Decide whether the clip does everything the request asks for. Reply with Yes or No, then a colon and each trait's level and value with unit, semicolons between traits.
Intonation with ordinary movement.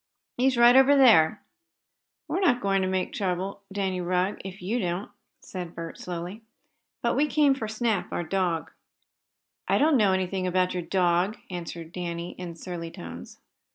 Yes: average, 3.9 semitones